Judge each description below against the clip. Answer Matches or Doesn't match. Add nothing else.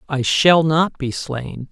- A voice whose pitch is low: Doesn't match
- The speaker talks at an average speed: Matches